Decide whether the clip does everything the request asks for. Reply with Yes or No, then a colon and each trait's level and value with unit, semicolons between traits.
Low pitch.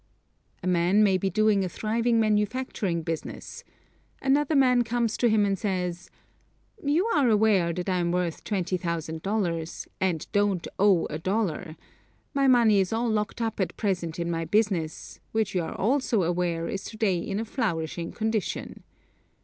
No: high, 195 Hz